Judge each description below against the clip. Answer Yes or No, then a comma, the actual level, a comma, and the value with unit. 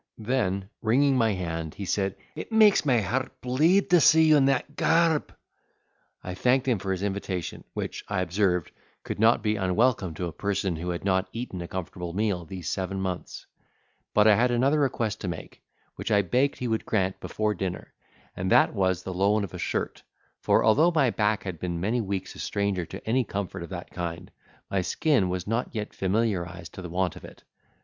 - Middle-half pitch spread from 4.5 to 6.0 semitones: Yes, average, 4.9 semitones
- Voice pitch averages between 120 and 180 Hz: No, low, 100 Hz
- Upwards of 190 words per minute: Yes, average, 200 wpm